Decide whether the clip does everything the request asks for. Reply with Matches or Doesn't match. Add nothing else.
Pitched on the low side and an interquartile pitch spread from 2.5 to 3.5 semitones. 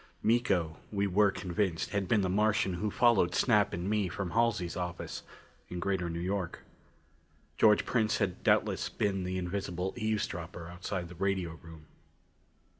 Matches